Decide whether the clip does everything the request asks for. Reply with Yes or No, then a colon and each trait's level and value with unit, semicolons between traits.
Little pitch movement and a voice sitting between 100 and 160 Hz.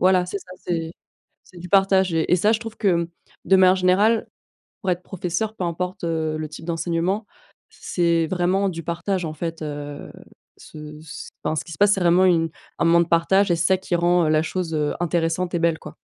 No: narrow, 2.3 semitones; medium, 175 Hz